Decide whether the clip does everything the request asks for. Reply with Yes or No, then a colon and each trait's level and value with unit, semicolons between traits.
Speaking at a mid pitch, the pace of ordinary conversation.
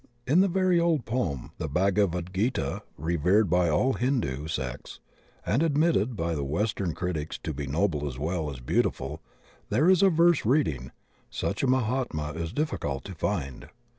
No: very low, 90 Hz; average, 165 wpm